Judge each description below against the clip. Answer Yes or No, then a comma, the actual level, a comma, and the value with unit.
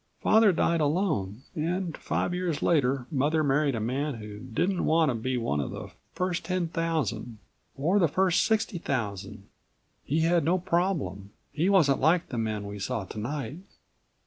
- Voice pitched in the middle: Yes, medium, 150 Hz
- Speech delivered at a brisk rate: No, average, 165 wpm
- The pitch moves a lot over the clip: Yes, wide, 6.4 semitones